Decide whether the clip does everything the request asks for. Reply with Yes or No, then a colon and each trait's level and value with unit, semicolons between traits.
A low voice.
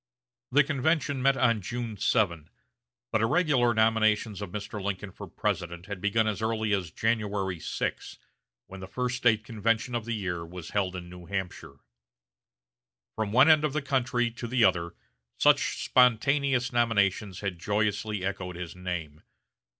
Yes: low, 105 Hz